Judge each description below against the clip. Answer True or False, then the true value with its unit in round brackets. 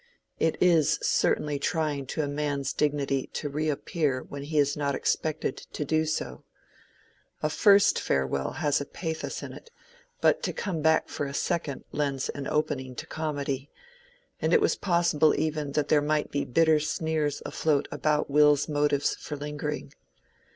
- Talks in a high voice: False (150 Hz)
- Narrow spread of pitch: True (1.8 semitones)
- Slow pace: False (160 wpm)